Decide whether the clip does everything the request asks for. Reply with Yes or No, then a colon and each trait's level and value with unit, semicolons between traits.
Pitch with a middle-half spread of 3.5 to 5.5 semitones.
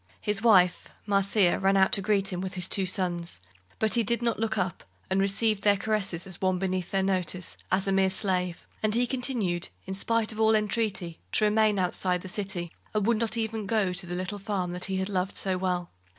No: average, 2.7 semitones